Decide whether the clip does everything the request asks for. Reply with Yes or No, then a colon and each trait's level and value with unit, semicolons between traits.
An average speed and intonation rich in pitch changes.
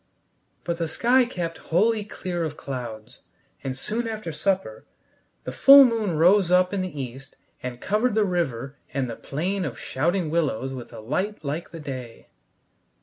Yes: average, 165 wpm; wide, 6.9 semitones